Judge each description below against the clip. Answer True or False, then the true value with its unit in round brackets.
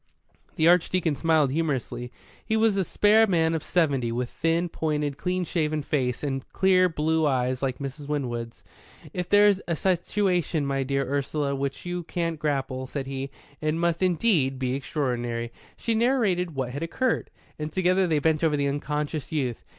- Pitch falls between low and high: True (155 Hz)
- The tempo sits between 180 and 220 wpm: False (170 wpm)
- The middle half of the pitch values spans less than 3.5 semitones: False (4.5 semitones)